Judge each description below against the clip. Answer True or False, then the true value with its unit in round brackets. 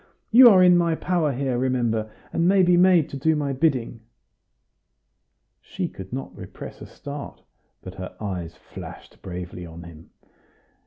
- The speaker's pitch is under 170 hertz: True (135 Hz)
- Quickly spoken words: False (155 wpm)